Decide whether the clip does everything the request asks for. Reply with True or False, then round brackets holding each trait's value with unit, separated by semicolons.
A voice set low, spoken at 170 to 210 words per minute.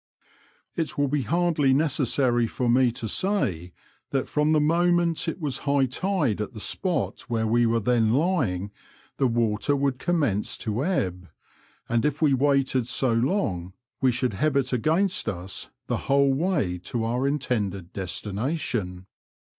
False (130 Hz; 155 wpm)